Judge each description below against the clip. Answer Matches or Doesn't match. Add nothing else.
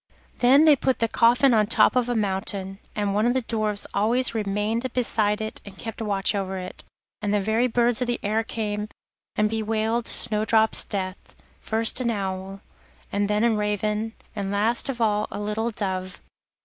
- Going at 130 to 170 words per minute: Doesn't match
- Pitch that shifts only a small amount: Matches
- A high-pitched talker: Matches